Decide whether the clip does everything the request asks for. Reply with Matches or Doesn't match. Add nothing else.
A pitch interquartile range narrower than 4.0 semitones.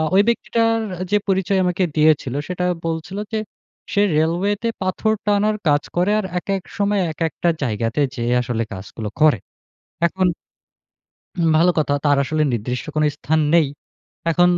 Doesn't match